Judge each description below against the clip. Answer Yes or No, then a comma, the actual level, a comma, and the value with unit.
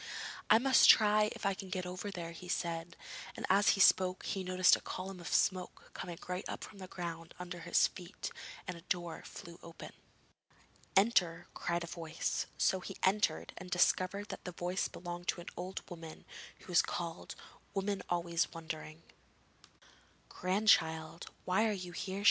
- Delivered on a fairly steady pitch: Yes, narrow, 2.1 semitones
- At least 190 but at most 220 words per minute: No, average, 170 wpm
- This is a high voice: No, medium, 180 Hz